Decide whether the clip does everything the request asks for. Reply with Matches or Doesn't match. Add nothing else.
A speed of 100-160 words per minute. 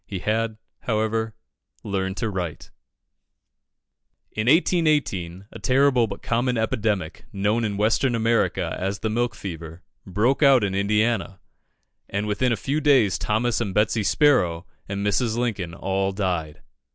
Matches